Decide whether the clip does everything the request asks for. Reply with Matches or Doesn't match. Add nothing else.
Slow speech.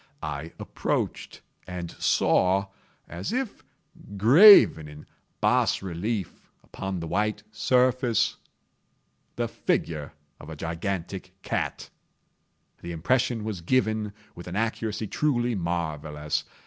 Matches